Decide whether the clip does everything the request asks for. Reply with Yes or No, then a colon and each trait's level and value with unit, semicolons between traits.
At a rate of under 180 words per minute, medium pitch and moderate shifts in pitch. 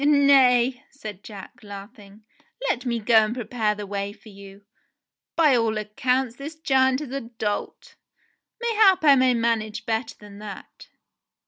No: average, 150 wpm; high, 235 Hz; average, 4.0 semitones